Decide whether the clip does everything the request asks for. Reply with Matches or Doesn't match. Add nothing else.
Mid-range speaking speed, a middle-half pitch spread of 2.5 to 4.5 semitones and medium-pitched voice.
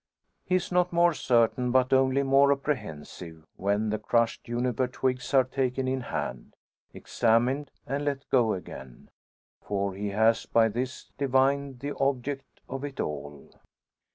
Doesn't match